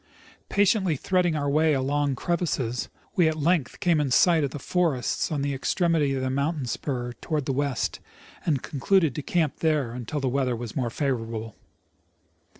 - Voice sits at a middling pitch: Yes, medium, 145 Hz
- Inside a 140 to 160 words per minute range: No, average, 175 wpm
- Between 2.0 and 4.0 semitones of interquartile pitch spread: Yes, average, 3.7 semitones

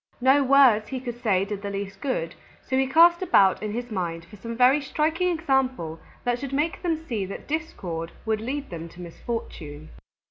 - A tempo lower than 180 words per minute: No, average, 190 wpm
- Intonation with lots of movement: Yes, wide, 6.3 semitones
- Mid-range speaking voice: No, high, 240 Hz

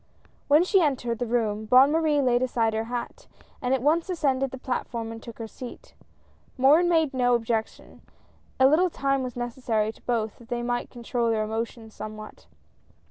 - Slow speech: No, average, 185 wpm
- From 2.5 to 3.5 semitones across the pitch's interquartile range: Yes, average, 3.2 semitones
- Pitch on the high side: Yes, high, 245 Hz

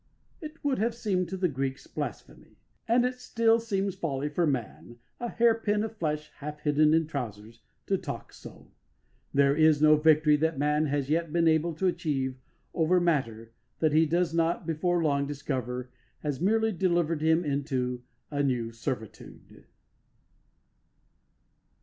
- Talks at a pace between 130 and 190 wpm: Yes, average, 155 wpm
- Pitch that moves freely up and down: No, average, 4.3 semitones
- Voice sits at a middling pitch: Yes, medium, 155 Hz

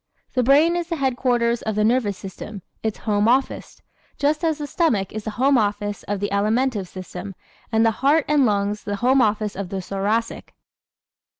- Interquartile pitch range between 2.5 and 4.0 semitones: No, average, 4.6 semitones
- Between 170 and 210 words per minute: Yes, average, 185 wpm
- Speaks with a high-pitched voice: Yes, high, 225 Hz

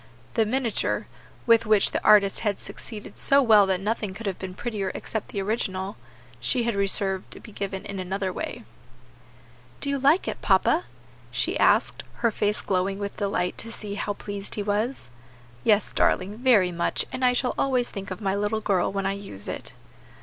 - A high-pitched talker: Yes, high, 205 Hz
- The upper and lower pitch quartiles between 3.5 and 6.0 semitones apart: No, average, 2.8 semitones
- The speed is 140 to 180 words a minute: No, average, 190 wpm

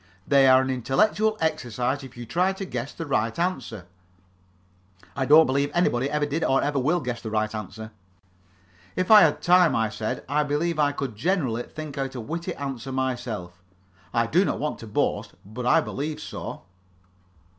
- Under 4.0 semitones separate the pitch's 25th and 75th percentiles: No, average, 4.9 semitones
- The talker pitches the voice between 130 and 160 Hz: Yes, low, 135 Hz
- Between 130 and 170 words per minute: No, average, 180 wpm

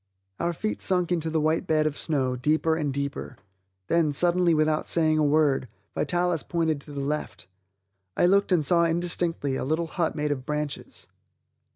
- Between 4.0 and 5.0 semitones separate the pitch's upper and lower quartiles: No, narrow, 2.6 semitones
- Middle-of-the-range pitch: Yes, medium, 155 Hz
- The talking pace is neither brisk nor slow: Yes, average, 175 wpm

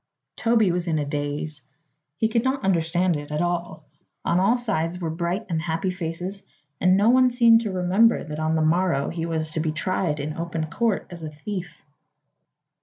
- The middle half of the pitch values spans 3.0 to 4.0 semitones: Yes, average, 3.7 semitones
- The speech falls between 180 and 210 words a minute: Yes, average, 190 wpm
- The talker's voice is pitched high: No, medium, 175 Hz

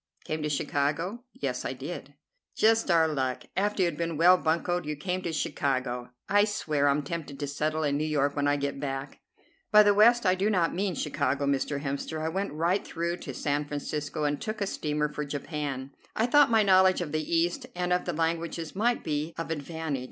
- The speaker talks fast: Yes, fast, 210 wpm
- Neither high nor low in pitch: Yes, medium, 155 Hz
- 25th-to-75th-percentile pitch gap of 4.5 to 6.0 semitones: No, average, 4.0 semitones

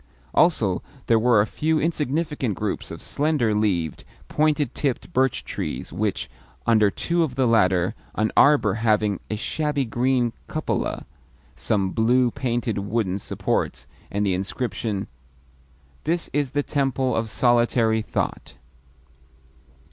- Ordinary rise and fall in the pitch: Yes, average, 4.7 semitones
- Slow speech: Yes, slow, 125 wpm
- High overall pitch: No, low, 115 Hz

